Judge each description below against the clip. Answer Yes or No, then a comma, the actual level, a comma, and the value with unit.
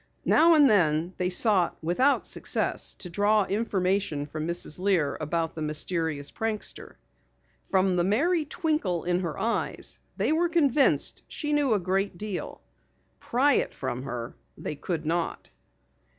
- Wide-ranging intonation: Yes, wide, 6.1 semitones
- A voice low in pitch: No, medium, 185 Hz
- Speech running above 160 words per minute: No, average, 145 wpm